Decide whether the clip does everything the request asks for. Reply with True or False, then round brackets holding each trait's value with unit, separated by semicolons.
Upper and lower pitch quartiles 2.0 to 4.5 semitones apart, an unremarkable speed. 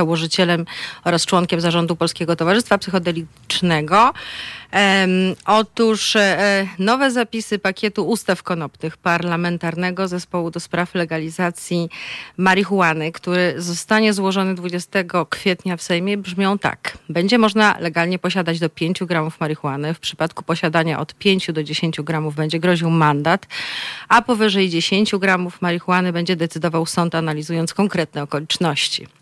True (2.7 semitones; 125 wpm)